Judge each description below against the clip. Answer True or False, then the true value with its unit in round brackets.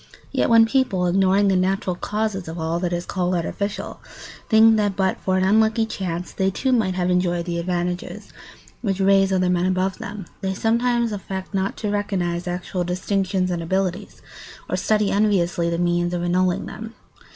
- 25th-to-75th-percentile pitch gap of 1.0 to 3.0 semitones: True (2.6 semitones)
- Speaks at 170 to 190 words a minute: True (175 wpm)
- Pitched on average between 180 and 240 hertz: True (190 Hz)